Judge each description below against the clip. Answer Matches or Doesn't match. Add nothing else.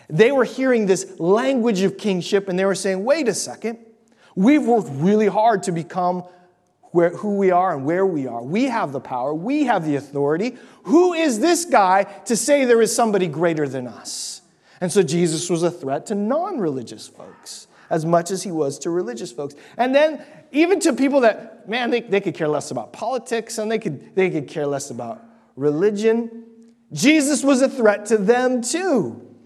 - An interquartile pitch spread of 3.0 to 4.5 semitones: Doesn't match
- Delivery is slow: Doesn't match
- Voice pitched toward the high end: Matches